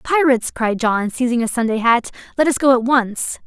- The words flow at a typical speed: No, fast, 210 wpm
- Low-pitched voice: No, high, 245 Hz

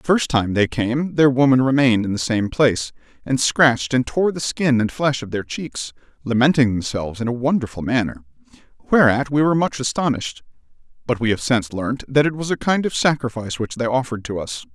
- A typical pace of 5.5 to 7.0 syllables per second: Yes, 5.8 syllables/s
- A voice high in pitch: No, low, 125 Hz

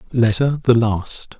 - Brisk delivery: No, slow, 130 wpm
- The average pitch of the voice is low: Yes, low, 115 Hz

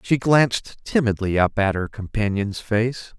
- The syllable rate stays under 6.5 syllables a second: Yes, 4.2 syllables/s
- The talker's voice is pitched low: Yes, low, 110 Hz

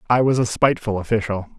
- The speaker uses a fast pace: No, average, 190 wpm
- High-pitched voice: No, low, 110 Hz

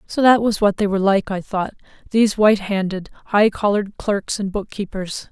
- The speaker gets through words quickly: No, average, 190 wpm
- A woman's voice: Yes, female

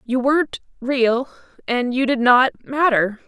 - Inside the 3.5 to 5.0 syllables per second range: Yes, 4.2 syllables/s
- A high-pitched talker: Yes, very high, 255 Hz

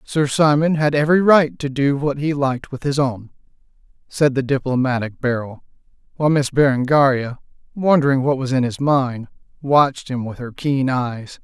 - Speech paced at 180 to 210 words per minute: No, average, 170 wpm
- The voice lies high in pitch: No, low, 135 Hz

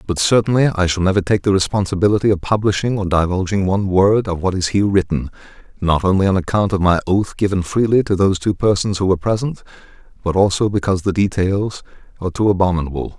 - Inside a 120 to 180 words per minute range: No, average, 195 wpm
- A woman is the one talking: No, male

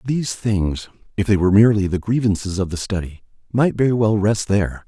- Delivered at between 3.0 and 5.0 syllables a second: No, 6.0 syllables/s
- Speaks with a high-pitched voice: No, low, 105 Hz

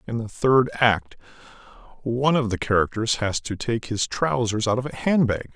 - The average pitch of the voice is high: No, low, 115 Hz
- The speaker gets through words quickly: No, average, 185 wpm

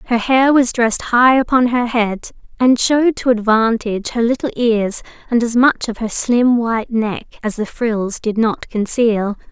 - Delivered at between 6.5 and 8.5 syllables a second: No, 4.6 syllables/s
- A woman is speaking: Yes, female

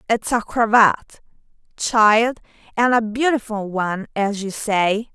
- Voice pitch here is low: No, high, 220 Hz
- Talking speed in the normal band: No, slow, 130 wpm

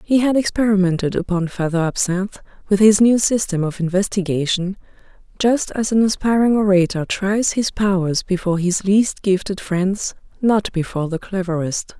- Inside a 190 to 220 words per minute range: No, average, 145 wpm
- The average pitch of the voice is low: No, high, 195 Hz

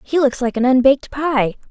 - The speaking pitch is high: Yes, very high, 260 Hz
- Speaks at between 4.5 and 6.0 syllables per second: Yes, 5.4 syllables/s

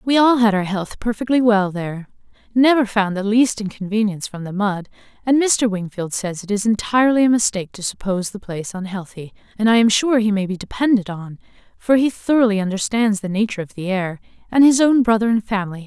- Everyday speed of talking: No, fast, 220 wpm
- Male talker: No, female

